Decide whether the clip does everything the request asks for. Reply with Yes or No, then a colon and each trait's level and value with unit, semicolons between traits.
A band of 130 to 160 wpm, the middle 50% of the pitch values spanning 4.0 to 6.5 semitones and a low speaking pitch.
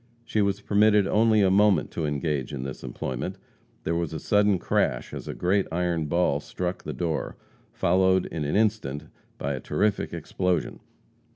No: average, 170 wpm; average, 4.9 semitones; very low, 90 Hz